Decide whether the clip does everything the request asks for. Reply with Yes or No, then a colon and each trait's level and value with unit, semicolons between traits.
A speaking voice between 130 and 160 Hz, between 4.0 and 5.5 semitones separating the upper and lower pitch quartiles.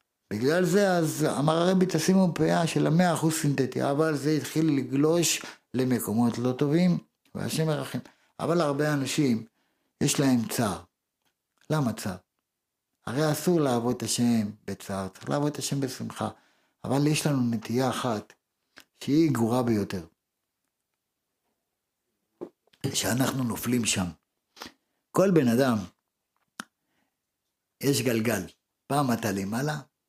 Yes: low, 135 Hz; average, 4.9 semitones